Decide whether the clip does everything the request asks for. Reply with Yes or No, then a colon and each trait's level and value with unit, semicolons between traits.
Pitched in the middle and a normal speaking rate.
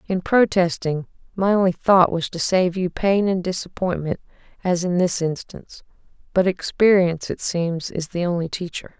Yes: medium, 180 Hz; average, 145 wpm